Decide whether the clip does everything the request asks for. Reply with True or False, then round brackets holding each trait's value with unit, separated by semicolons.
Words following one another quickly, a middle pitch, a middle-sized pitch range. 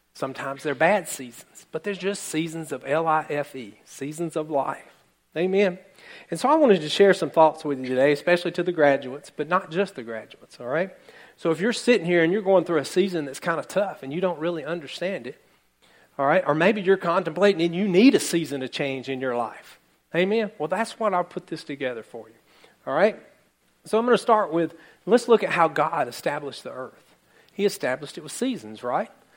True (215 wpm; 170 Hz; 4.9 semitones)